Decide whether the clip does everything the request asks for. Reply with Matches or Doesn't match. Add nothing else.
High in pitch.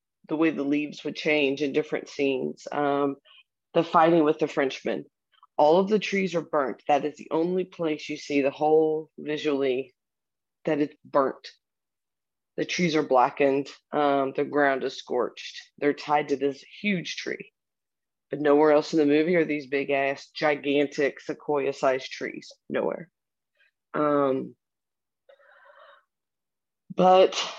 Doesn't match